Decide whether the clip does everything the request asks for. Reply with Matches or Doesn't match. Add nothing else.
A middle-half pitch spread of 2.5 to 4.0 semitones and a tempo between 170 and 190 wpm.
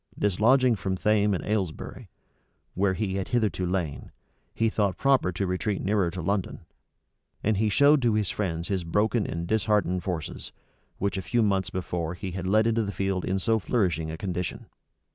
Matches